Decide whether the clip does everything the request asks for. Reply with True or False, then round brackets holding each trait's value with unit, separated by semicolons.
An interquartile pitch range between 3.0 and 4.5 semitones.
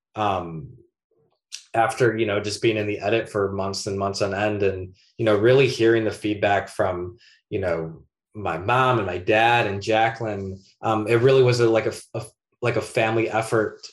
False (2.6 semitones)